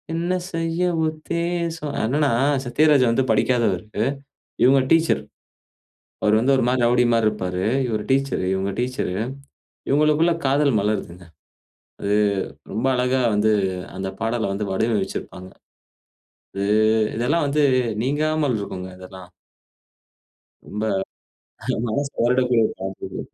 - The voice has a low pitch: Yes, low, 125 Hz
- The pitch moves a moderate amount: No, wide, 5.9 semitones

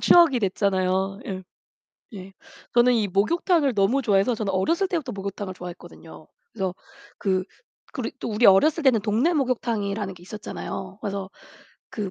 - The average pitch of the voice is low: No, high, 200 Hz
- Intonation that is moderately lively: Yes, average, 4.5 semitones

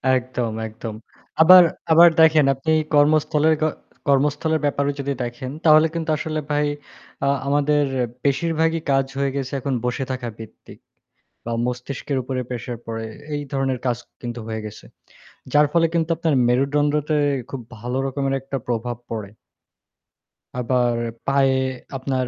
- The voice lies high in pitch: No, low, 135 Hz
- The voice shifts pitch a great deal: No, average, 3.2 semitones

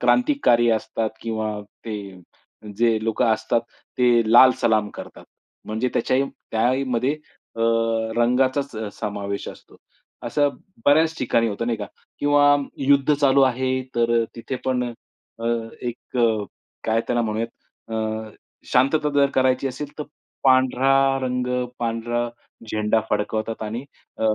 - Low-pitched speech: Yes, low, 120 Hz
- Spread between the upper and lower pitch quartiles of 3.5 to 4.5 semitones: No, average, 3.0 semitones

